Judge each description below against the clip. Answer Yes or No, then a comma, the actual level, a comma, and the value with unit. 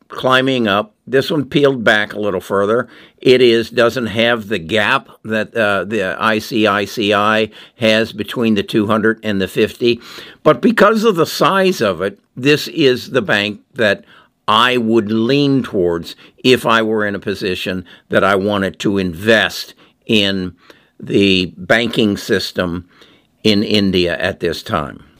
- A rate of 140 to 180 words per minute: Yes, average, 150 wpm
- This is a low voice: Yes, low, 110 Hz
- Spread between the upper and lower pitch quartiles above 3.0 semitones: Yes, average, 3.5 semitones